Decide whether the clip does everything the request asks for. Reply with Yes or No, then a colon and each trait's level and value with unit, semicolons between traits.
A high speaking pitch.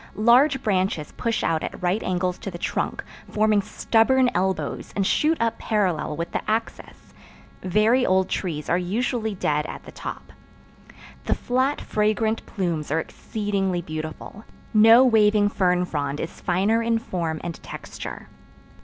Yes: high, 200 Hz